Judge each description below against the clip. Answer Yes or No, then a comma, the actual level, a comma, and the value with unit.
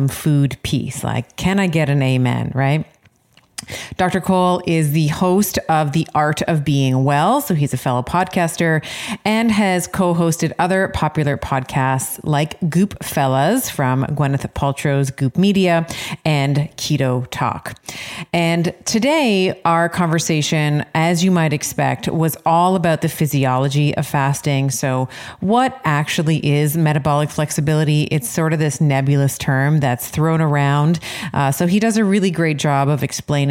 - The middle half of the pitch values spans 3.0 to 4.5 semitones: Yes, average, 3.6 semitones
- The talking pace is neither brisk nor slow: Yes, average, 150 wpm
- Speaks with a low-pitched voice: No, medium, 155 Hz